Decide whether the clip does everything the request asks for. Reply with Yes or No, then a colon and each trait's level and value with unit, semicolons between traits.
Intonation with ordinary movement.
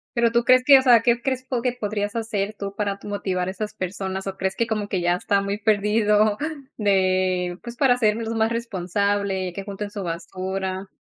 Yes: average, 3.1 semitones